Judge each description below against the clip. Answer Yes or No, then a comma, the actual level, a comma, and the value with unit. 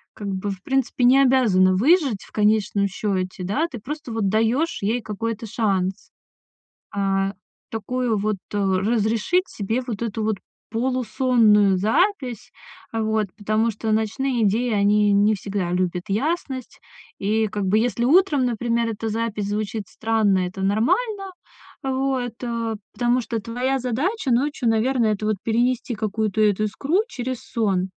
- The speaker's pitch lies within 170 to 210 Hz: No, high, 220 Hz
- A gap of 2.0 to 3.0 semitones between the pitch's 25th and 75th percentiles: No, average, 3.5 semitones